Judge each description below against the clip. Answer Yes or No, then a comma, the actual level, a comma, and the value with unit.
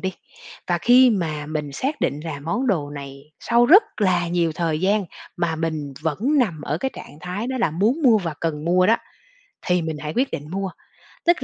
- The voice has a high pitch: No, medium, 175 Hz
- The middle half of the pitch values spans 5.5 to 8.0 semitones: Yes, wide, 6.0 semitones